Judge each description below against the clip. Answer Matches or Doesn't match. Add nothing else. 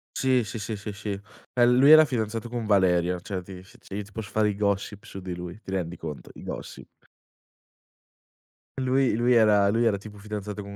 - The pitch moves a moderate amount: Matches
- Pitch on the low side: Matches